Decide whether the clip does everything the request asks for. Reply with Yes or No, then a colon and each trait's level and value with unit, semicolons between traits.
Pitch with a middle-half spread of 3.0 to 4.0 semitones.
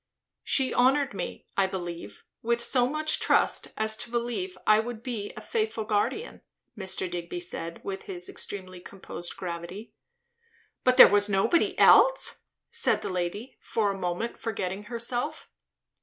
No: average, 4.7 semitones